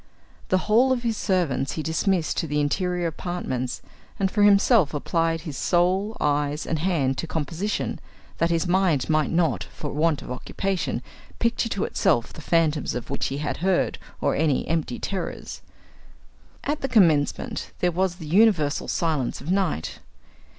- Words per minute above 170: No, average, 160 wpm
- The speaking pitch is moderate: Yes, medium, 165 Hz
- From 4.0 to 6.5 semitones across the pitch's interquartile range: Yes, average, 4.4 semitones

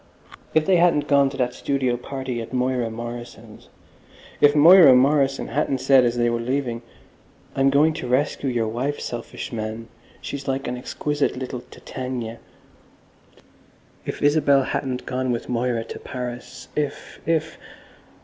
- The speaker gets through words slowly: Yes, slow, 130 wpm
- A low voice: Yes, low, 130 Hz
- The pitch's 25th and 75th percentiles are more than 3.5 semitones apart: No, average, 2.7 semitones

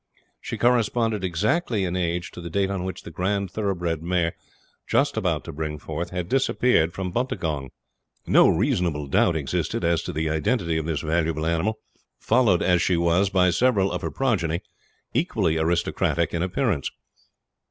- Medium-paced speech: Yes, average, 165 wpm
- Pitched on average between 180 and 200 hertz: No, very low, 90 Hz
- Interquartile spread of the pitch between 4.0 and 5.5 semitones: No, average, 3.6 semitones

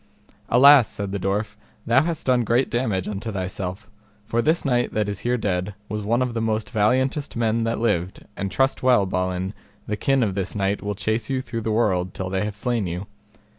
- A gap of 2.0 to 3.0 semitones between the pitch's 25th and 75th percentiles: No, average, 3.7 semitones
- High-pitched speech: No, low, 110 Hz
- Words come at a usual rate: No, fast, 210 wpm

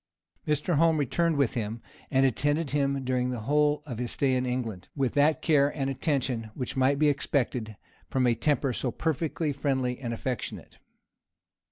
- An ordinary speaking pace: Yes, average, 170 wpm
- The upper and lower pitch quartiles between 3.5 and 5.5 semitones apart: No, average, 2.9 semitones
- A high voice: No, low, 135 Hz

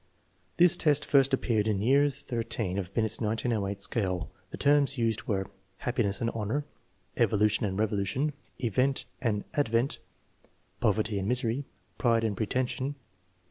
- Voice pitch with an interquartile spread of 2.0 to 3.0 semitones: No, average, 4.2 semitones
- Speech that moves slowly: No, average, 145 wpm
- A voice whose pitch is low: Yes, low, 115 Hz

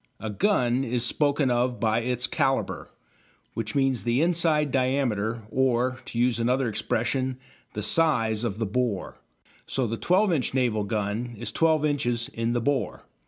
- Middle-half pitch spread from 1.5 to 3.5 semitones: Yes, average, 2.9 semitones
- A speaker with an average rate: Yes, average, 160 wpm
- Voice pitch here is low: Yes, low, 125 Hz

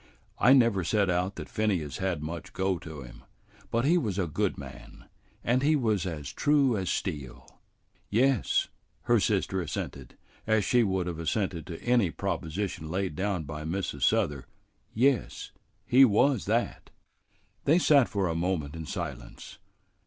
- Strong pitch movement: Yes, wide, 5.9 semitones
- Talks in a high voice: No, very low, 95 Hz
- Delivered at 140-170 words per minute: Yes, average, 155 wpm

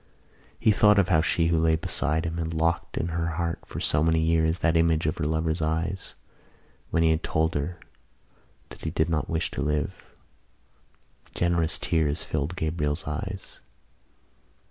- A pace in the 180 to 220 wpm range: No, average, 165 wpm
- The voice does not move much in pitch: Yes, narrow, 1.1 semitones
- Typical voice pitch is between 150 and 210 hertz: No, very low, 80 Hz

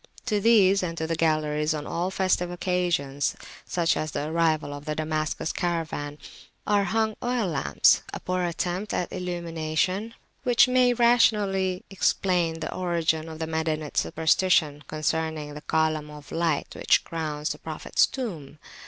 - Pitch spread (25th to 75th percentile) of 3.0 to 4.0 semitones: Yes, average, 3.3 semitones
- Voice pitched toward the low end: No, medium, 165 Hz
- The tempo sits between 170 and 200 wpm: No, average, 150 wpm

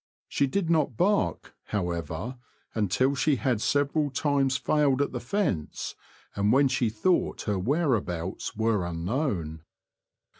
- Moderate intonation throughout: No, wide, 6.1 semitones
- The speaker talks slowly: Yes, slow, 125 wpm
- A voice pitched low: Yes, low, 130 Hz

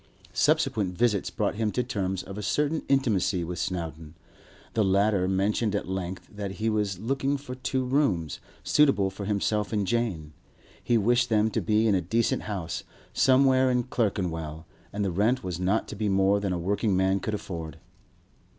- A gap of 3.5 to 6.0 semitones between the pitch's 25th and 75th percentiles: Yes, average, 3.9 semitones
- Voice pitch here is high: No, low, 100 Hz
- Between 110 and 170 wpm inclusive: No, average, 180 wpm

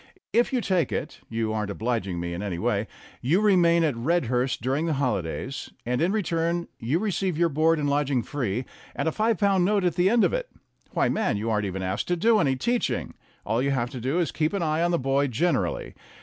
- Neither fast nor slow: No, fast, 235 wpm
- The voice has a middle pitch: Yes, medium, 145 Hz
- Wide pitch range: Yes, wide, 6.9 semitones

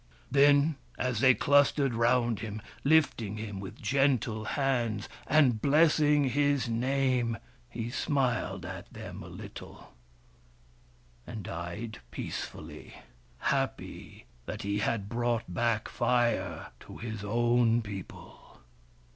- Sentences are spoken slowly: Yes, slow, 110 wpm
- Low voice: Yes, low, 120 Hz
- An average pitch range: Yes, average, 4.0 semitones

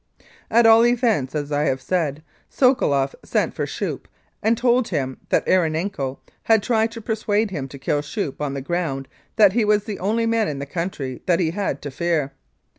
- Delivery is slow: No, average, 190 wpm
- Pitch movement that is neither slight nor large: No, wide, 7.5 semitones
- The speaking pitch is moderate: Yes, medium, 175 Hz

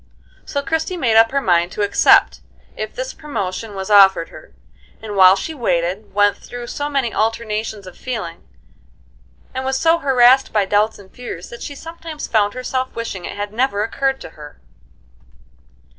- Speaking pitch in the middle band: No, high, 225 Hz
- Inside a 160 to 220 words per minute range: Yes, average, 170 wpm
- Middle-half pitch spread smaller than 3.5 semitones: No, average, 5.0 semitones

